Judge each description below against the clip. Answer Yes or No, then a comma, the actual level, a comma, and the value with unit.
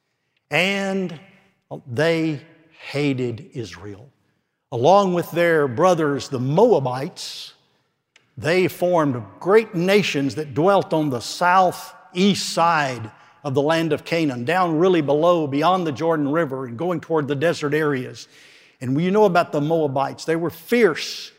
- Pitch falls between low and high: Yes, medium, 160 Hz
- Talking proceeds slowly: Yes, slow, 130 wpm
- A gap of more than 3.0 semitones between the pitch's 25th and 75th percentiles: Yes, average, 3.9 semitones